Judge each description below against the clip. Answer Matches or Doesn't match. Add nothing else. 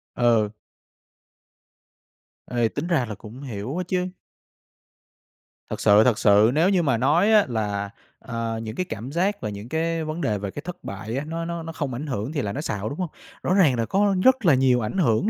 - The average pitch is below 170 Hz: Matches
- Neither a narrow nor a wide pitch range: Doesn't match